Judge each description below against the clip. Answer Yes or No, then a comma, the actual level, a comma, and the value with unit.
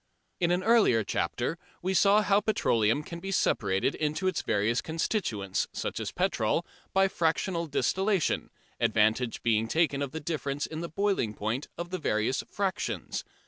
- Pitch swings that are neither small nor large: No, wide, 8.3 semitones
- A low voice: No, medium, 160 Hz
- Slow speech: No, average, 155 wpm